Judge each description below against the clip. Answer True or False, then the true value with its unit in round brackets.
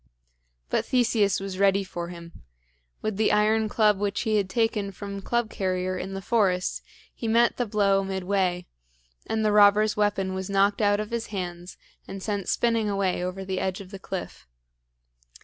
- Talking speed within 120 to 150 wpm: False (175 wpm)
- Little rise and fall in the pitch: True (2.1 semitones)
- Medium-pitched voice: False (200 Hz)